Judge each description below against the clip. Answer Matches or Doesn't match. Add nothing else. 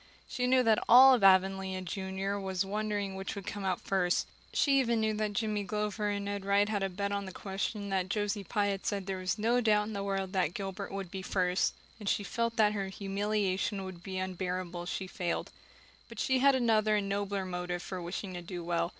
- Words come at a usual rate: Doesn't match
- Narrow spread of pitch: Matches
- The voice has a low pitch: Doesn't match